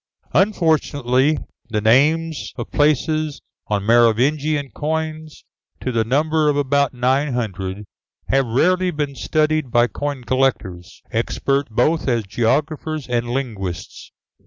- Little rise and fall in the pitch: No, average, 4.4 semitones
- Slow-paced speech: Yes, slow, 115 wpm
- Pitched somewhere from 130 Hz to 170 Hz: Yes, low, 135 Hz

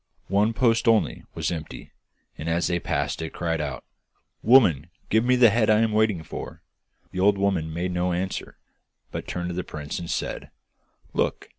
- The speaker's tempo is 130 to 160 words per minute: No, average, 180 wpm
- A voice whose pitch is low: Yes, very low, 90 Hz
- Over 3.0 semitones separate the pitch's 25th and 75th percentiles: Yes, average, 4.6 semitones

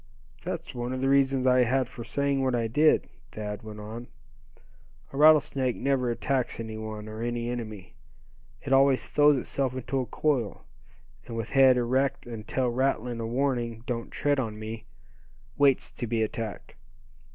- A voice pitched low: Yes, low, 125 Hz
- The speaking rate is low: No, average, 165 wpm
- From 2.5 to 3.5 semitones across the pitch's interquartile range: Yes, average, 2.9 semitones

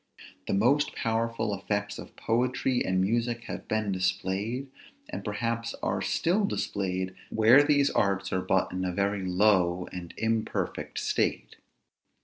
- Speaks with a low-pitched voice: Yes, low, 105 Hz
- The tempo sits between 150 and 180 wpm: No, slow, 135 wpm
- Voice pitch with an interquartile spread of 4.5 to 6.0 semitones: No, average, 3.8 semitones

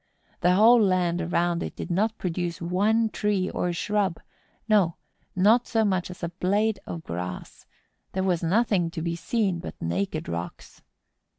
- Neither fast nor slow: Yes, average, 160 wpm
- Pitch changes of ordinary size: Yes, average, 3.5 semitones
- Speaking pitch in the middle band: Yes, medium, 180 Hz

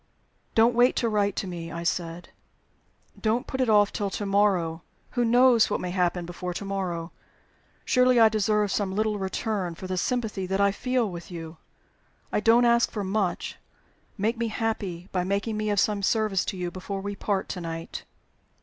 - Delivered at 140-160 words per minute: No, average, 185 wpm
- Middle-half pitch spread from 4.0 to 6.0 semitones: No, average, 3.5 semitones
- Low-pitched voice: No, high, 200 Hz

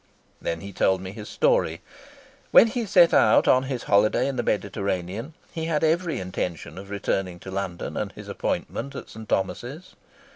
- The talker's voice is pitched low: Yes, low, 110 Hz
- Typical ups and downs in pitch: No, wide, 8.5 semitones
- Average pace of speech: Yes, average, 175 wpm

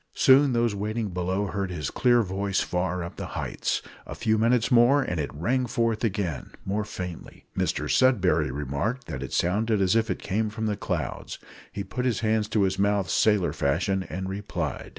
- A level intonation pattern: No, average, 3.8 semitones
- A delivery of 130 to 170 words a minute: No, average, 190 wpm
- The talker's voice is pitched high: No, low, 100 Hz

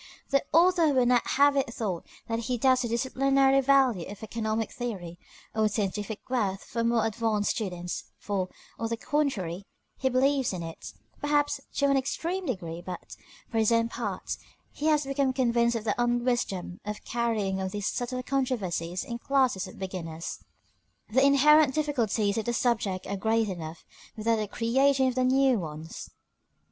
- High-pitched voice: Yes, high, 235 Hz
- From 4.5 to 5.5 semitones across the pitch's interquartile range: Yes, average, 4.9 semitones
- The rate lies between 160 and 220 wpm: Yes, average, 165 wpm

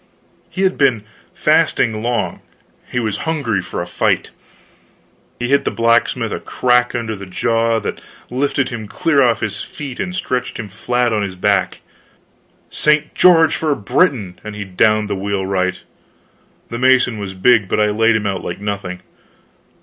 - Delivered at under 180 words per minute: Yes, average, 165 wpm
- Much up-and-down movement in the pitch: No, average, 3.9 semitones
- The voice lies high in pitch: No, low, 115 Hz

